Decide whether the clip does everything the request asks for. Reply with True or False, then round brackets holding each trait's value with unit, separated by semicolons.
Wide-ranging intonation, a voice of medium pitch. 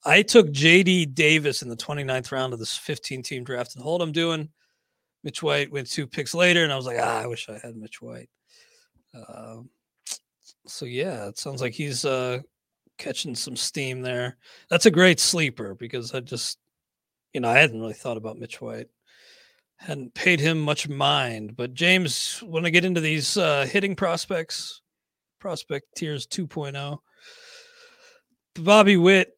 True (5.8 semitones; 145 Hz)